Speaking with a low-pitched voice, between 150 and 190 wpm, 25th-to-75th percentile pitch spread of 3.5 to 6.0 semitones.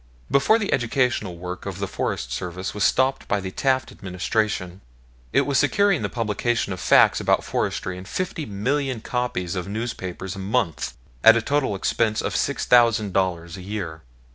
Yes: low, 105 Hz; average, 165 wpm; average, 5.2 semitones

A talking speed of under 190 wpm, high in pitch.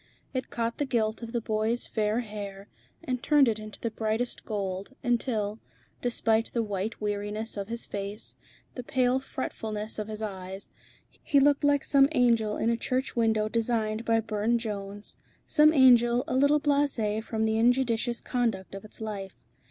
Yes: average, 165 wpm; high, 225 Hz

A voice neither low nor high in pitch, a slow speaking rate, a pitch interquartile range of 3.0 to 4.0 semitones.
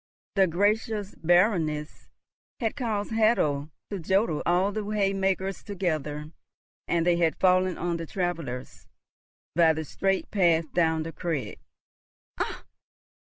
Yes: medium, 175 Hz; slow, 125 wpm; average, 3.6 semitones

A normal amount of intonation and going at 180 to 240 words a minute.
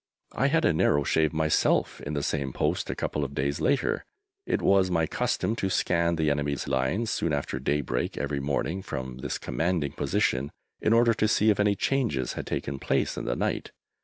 No: wide, 5.7 semitones; average, 195 wpm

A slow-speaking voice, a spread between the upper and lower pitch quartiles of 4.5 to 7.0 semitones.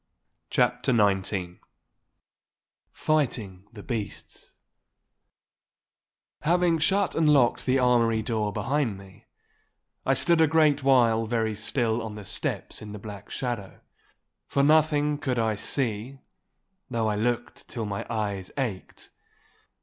Yes: slow, 120 wpm; average, 5.0 semitones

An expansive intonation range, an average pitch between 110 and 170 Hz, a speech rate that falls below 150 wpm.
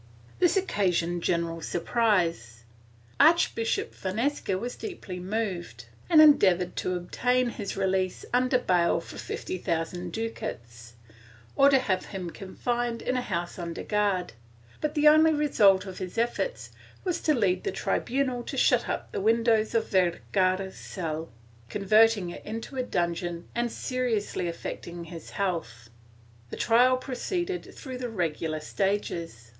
No: wide, 6.0 semitones; high, 195 Hz; average, 140 wpm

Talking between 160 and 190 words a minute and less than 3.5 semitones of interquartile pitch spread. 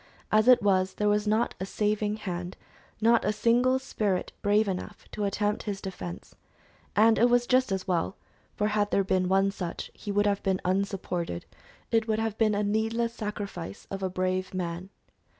Yes: average, 185 wpm; narrow, 2.5 semitones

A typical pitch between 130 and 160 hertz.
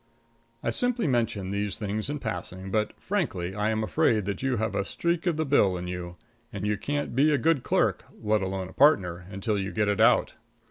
No: low, 105 Hz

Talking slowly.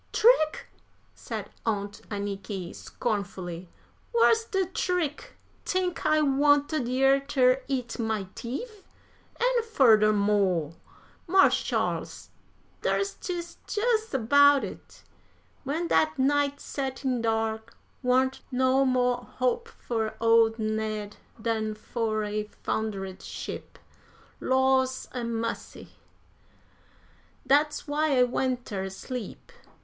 Yes: slow, 105 wpm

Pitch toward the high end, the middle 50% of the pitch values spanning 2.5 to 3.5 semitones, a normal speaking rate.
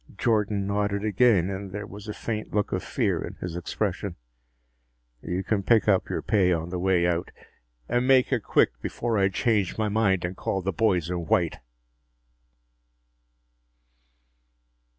No: low, 100 Hz; average, 3.0 semitones; average, 155 wpm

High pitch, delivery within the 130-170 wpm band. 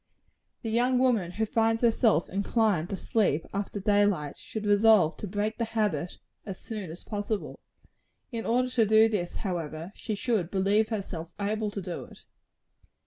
Yes: high, 205 Hz; average, 165 wpm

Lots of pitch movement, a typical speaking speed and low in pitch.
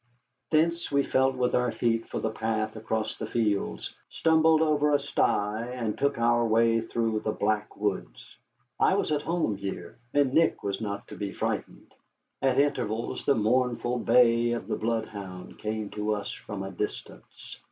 No: average, 3.7 semitones; average, 170 wpm; low, 115 Hz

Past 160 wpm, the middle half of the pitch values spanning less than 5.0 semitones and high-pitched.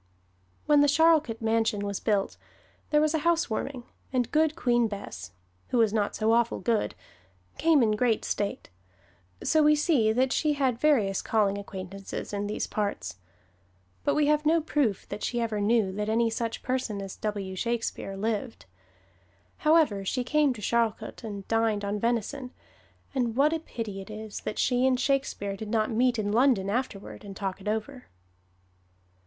Yes: average, 170 wpm; average, 4.5 semitones; high, 225 Hz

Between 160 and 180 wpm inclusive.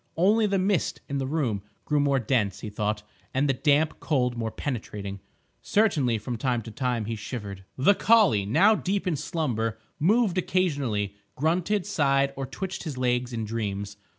Yes: average, 165 wpm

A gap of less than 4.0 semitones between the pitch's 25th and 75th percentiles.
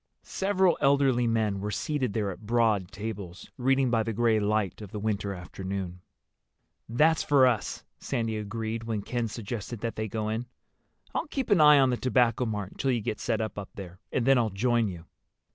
Yes: average, 3.4 semitones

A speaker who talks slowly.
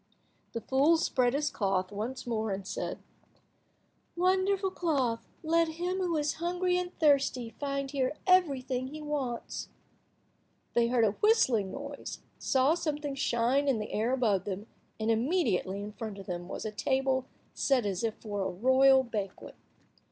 No: average, 155 wpm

